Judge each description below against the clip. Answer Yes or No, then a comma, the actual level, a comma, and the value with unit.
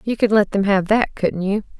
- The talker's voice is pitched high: Yes, high, 205 Hz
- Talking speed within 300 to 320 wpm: No, fast, 270 wpm